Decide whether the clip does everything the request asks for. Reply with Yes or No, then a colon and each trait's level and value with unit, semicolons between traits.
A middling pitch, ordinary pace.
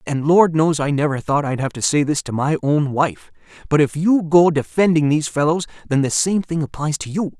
No: medium, 150 Hz; fast, 220 wpm